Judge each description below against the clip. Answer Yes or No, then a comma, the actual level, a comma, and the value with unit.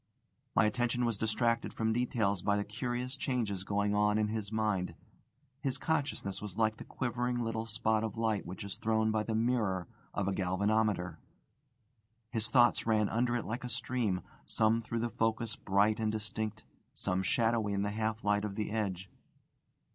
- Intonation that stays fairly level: Yes, narrow, 2.3 semitones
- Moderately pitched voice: No, low, 110 Hz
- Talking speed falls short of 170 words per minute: No, average, 175 wpm